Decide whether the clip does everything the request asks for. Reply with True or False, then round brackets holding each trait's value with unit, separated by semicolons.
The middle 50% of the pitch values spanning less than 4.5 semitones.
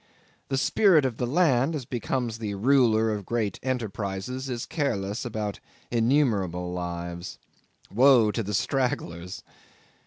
False (4.9 semitones)